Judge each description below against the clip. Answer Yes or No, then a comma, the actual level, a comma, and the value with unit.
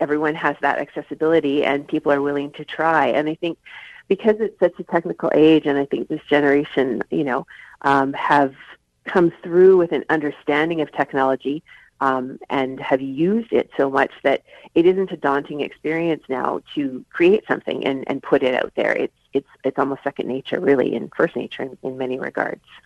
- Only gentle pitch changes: No, average, 3.5 semitones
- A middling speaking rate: Yes, average, 190 wpm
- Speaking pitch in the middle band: Yes, medium, 150 Hz